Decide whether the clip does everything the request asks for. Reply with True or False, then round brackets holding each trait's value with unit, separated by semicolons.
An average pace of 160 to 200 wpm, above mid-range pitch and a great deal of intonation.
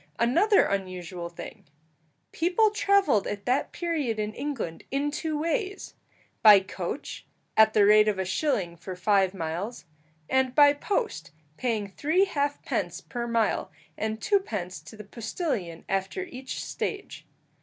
False (140 wpm; 225 Hz; 7.5 semitones)